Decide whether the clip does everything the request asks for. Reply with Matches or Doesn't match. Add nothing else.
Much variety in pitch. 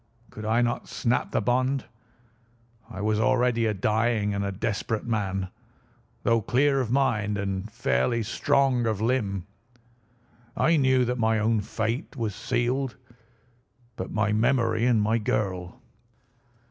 Doesn't match